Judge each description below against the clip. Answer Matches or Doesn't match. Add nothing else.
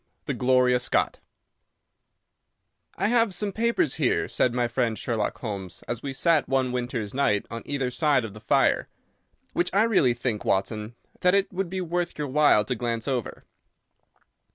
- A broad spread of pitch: Matches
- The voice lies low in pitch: Matches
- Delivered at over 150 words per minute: Matches